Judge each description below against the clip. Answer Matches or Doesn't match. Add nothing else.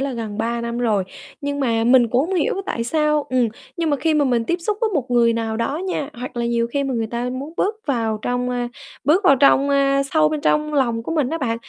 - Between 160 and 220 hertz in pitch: Doesn't match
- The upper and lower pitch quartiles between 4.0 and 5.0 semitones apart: Matches